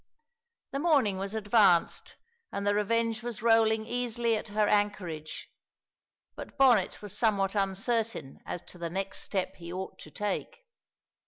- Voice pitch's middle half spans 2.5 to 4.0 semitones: Yes, average, 3.0 semitones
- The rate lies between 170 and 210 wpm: No, average, 145 wpm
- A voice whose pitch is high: Yes, high, 210 Hz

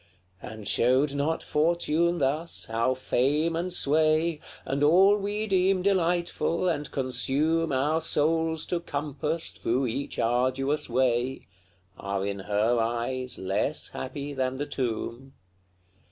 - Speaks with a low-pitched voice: No, medium, 145 Hz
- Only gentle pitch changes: No, average, 4.3 semitones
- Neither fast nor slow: No, slow, 125 wpm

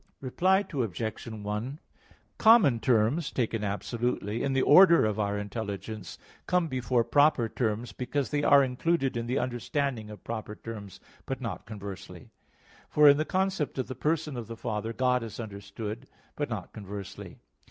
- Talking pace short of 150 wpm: No, average, 155 wpm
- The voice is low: Yes, low, 120 Hz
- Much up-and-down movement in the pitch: No, average, 4.9 semitones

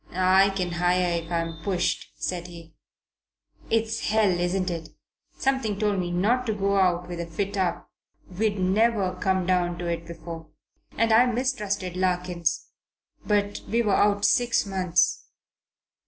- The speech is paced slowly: No, average, 150 wpm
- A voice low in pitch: No, medium, 185 Hz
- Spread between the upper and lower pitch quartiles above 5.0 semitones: No, average, 2.9 semitones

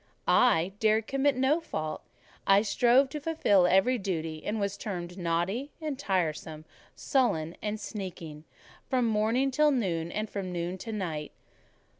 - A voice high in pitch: Yes, high, 200 Hz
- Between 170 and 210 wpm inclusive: No, average, 150 wpm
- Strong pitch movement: Yes, wide, 6.4 semitones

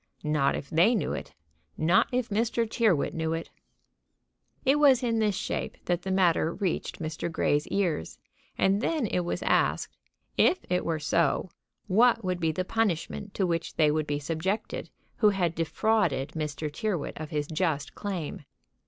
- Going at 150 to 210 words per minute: Yes, average, 165 wpm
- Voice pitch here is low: No, medium, 175 Hz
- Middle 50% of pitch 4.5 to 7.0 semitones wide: Yes, average, 5.0 semitones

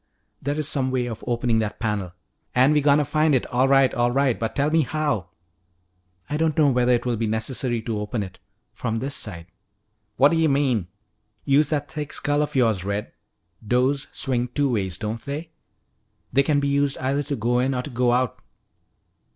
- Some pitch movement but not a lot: Yes, average, 3.8 semitones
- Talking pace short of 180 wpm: No, average, 200 wpm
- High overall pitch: No, low, 130 Hz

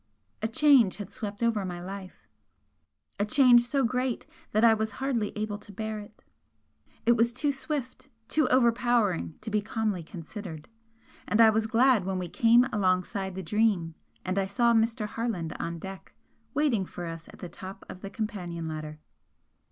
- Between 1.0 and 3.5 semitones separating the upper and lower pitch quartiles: No, average, 4.0 semitones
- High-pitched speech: Yes, high, 215 Hz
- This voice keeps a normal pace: Yes, average, 170 wpm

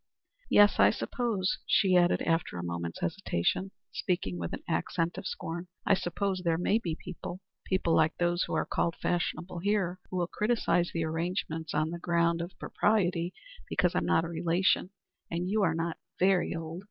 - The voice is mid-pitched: Yes, medium, 175 Hz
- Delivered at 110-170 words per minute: No, average, 180 wpm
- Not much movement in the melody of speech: Yes, narrow, 2.1 semitones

